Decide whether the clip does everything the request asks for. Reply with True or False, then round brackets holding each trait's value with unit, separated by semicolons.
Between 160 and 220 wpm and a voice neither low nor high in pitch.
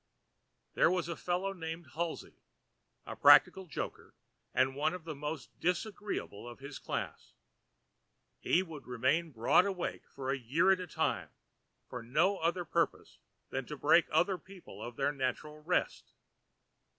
False (150 wpm; 160 Hz)